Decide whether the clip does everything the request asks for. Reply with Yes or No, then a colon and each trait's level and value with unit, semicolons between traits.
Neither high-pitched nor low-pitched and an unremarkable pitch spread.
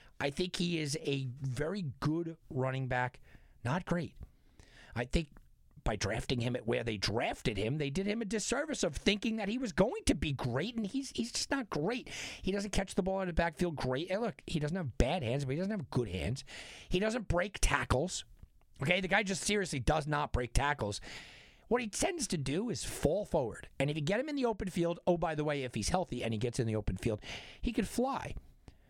No: medium, 155 Hz; wide, 7.5 semitones